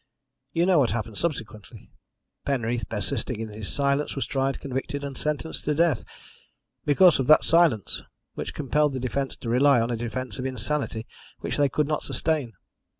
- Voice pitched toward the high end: No, low, 135 Hz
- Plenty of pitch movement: No, average, 4.0 semitones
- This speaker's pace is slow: No, average, 170 wpm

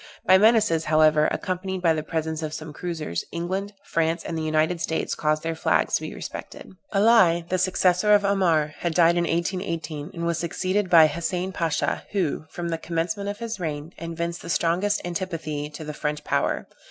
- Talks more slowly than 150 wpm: No, average, 185 wpm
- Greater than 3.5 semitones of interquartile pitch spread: No, average, 2.8 semitones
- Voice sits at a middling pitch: Yes, medium, 170 Hz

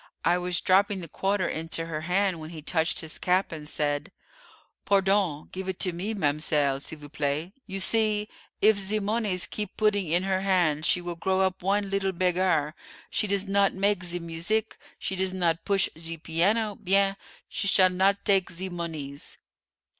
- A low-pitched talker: No, medium, 185 Hz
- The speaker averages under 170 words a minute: No, average, 180 wpm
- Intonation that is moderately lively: Yes, average, 3.1 semitones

